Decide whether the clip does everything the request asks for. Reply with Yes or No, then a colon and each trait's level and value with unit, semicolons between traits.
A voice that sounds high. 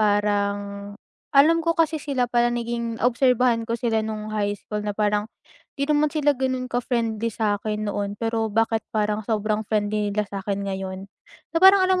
Yes: high, 220 Hz